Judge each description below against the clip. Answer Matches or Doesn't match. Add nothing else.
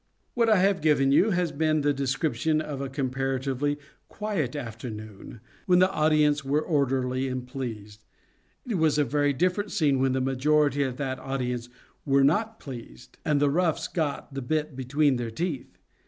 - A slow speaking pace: Doesn't match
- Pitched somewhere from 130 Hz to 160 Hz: Matches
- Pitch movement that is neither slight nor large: Matches